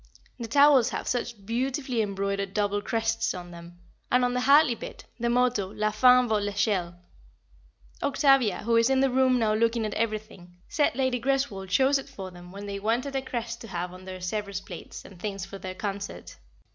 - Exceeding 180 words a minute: Yes, average, 195 wpm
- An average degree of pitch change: Yes, average, 4.1 semitones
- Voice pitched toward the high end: Yes, high, 220 Hz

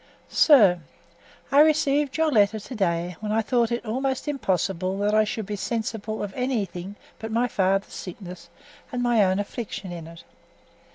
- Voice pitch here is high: Yes, high, 215 Hz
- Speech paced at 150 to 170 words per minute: Yes, average, 165 wpm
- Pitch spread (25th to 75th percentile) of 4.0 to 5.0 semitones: Yes, average, 4.4 semitones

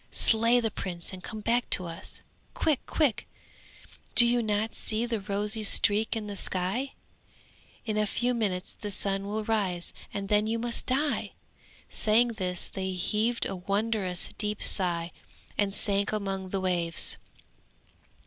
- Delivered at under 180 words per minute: Yes, average, 150 wpm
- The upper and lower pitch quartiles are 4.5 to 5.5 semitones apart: No, average, 3.1 semitones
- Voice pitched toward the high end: Yes, high, 210 Hz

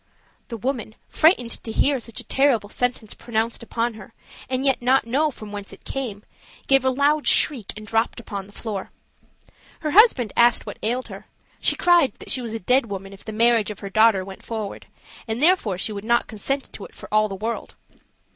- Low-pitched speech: No, high, 230 Hz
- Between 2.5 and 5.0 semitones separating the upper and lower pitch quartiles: Yes, average, 3.6 semitones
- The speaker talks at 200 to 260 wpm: Yes, fast, 205 wpm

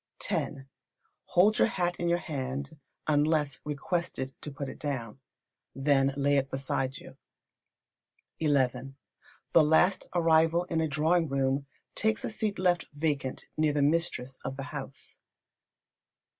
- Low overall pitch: No, medium, 145 Hz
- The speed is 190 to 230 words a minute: No, slow, 135 wpm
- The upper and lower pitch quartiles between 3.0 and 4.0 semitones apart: Yes, average, 3.5 semitones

